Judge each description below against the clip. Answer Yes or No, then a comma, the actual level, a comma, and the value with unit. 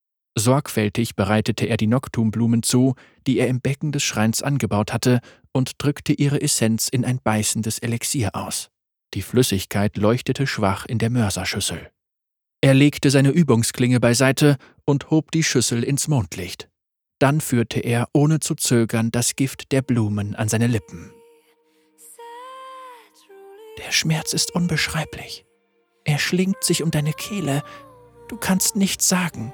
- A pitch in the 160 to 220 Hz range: No, low, 130 Hz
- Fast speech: No, average, 140 wpm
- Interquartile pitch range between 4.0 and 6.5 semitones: Yes, average, 5.2 semitones